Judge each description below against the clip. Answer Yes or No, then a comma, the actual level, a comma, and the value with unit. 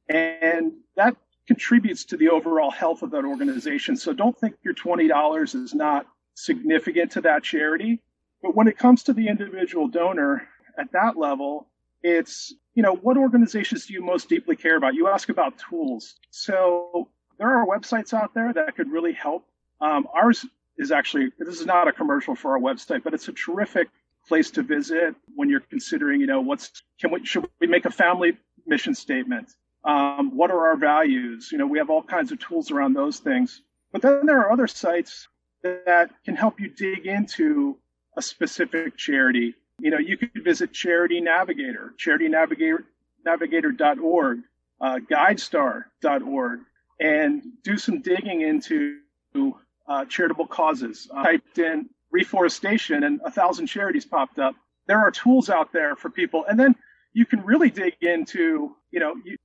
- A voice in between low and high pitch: No, very high, 250 Hz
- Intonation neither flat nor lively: No, wide, 9.0 semitones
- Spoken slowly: No, average, 170 wpm